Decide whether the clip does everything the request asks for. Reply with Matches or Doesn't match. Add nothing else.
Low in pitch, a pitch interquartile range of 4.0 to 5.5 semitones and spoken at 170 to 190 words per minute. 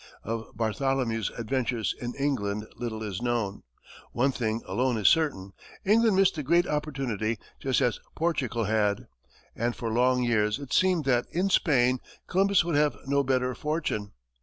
Doesn't match